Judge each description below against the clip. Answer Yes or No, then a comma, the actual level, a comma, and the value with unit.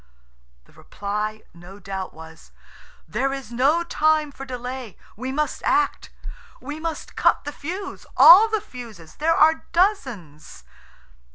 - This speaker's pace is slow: Yes, slow, 125 wpm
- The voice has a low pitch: No, very high, 265 Hz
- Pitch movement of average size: No, wide, 7.3 semitones